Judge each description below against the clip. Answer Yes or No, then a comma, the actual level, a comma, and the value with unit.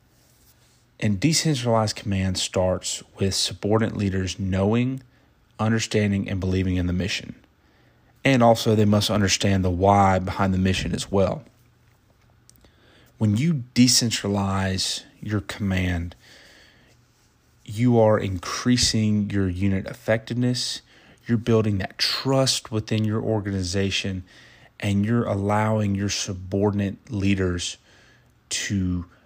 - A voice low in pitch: Yes, low, 105 Hz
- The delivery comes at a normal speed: No, slow, 105 wpm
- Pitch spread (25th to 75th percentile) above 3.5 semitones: No, average, 3.0 semitones